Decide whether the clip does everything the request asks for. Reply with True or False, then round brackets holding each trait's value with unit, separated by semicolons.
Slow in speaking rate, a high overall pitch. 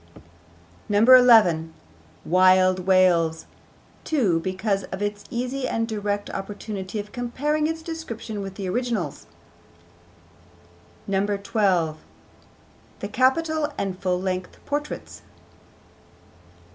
True (90 wpm; 205 Hz)